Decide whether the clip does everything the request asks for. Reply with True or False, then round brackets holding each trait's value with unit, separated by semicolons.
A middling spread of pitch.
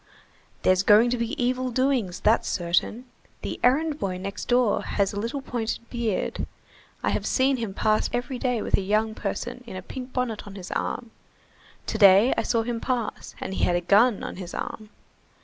True (3.9 semitones)